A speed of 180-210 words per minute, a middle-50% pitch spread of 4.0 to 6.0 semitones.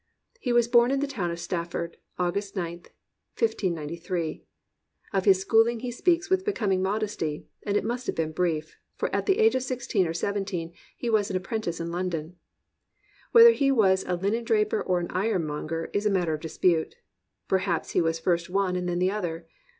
Yes: average, 190 wpm; average, 4.9 semitones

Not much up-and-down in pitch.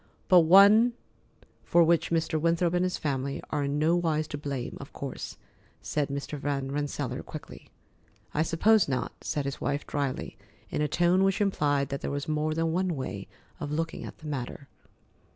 No: average, 3.2 semitones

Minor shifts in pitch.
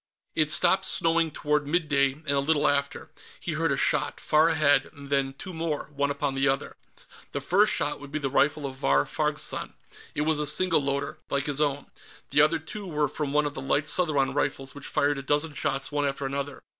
Yes: narrow, 1.7 semitones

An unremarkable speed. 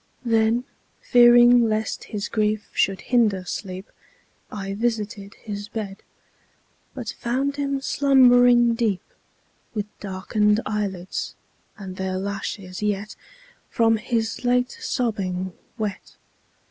No: slow, 110 wpm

